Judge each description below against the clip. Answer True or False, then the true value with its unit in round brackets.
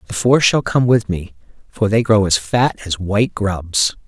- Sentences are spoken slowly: False (205 wpm)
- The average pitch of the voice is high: False (105 Hz)